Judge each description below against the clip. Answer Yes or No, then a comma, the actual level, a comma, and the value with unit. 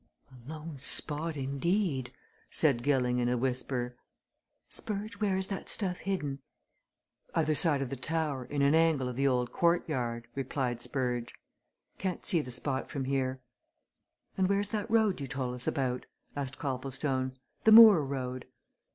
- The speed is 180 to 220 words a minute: No, average, 150 wpm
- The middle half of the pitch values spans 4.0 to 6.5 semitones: Yes, average, 4.4 semitones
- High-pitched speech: No, medium, 140 Hz